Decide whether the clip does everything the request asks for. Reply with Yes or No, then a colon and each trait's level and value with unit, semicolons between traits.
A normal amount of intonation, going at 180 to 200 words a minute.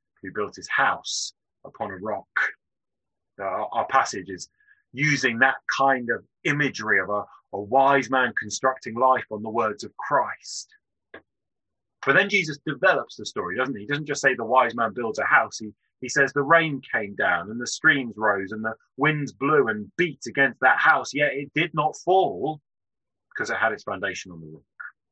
Yes: average, 4.8 semitones; average, 190 wpm